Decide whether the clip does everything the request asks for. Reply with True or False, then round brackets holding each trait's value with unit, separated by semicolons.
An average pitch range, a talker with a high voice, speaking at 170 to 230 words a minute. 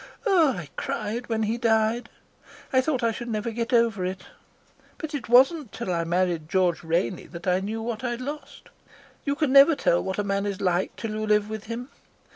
True (4.5 semitones; 220 Hz; 205 wpm)